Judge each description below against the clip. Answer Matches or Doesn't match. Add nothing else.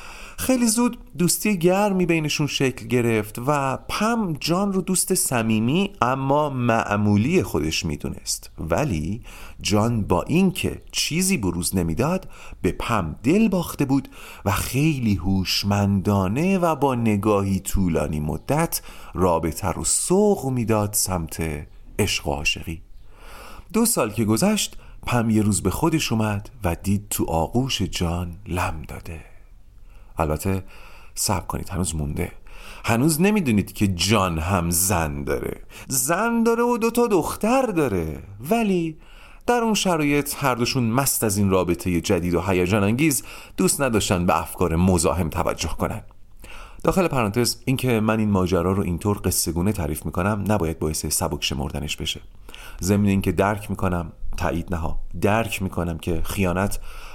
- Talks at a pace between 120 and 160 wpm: Matches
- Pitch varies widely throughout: Matches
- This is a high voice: Doesn't match